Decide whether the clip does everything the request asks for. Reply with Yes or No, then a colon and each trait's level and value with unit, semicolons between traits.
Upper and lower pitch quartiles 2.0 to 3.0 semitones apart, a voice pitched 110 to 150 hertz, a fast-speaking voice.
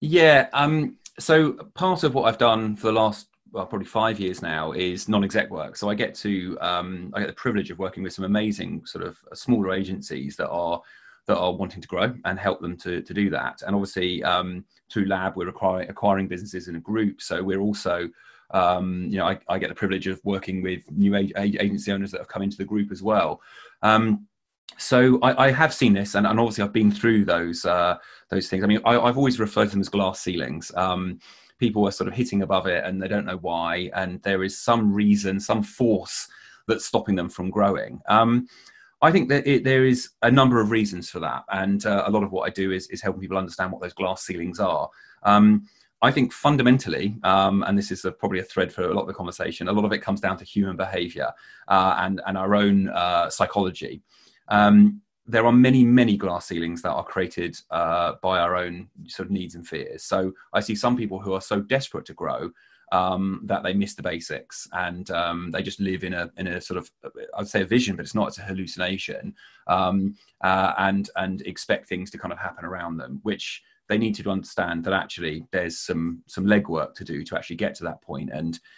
No: average, 2.7 semitones; low, 100 Hz; fast, 225 wpm